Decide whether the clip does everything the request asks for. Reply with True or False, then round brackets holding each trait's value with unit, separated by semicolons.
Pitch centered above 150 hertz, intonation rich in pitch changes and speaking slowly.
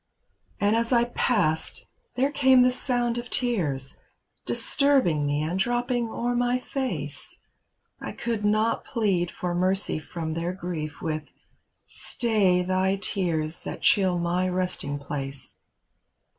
True (190 Hz; 6.8 semitones; 130 wpm)